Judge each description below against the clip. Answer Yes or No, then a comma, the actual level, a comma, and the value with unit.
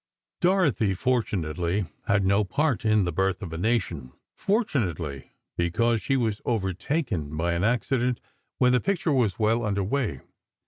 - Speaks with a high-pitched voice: No, low, 105 Hz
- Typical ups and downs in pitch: No, wide, 5.9 semitones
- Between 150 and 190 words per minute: No, average, 140 wpm